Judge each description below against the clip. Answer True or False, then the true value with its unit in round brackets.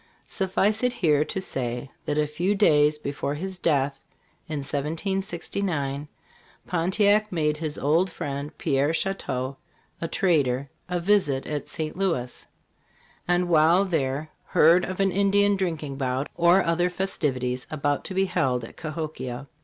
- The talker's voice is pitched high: False (155 Hz)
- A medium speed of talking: True (145 wpm)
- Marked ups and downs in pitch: False (4.8 semitones)